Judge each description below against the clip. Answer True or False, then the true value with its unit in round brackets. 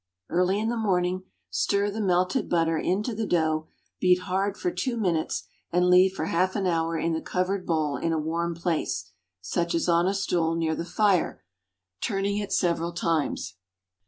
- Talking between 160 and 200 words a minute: True (170 wpm)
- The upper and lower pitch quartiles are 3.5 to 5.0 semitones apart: False (2.9 semitones)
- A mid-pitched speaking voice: True (175 Hz)